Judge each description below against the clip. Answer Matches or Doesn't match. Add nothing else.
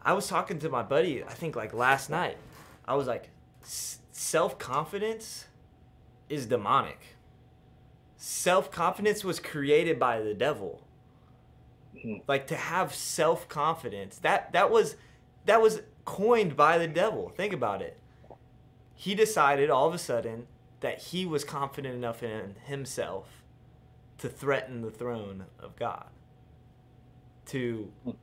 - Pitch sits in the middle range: Doesn't match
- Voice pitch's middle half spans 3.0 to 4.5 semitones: Doesn't match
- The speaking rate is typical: Doesn't match